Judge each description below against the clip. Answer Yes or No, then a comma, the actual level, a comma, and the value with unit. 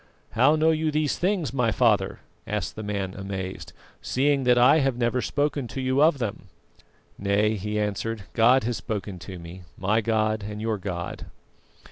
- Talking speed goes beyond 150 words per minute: Yes, average, 170 wpm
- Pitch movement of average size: Yes, average, 4.6 semitones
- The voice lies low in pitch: Yes, low, 110 Hz